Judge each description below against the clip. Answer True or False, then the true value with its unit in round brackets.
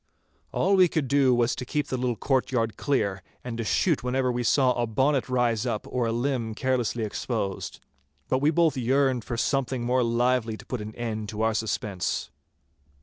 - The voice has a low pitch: True (125 Hz)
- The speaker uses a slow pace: False (190 wpm)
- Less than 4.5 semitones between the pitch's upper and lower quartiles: True (2.7 semitones)